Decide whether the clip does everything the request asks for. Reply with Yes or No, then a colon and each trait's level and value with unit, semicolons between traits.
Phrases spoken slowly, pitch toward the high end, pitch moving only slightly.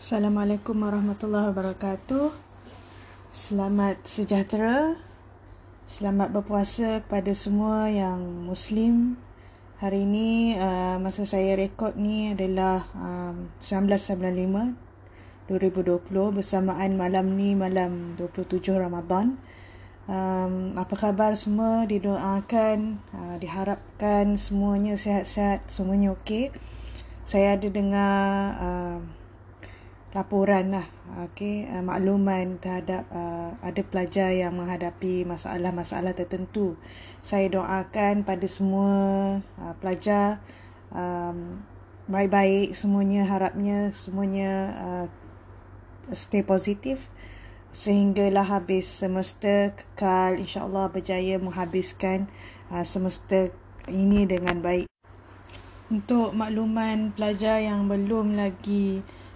Yes: slow, 85 wpm; high, 195 Hz; narrow, 2.0 semitones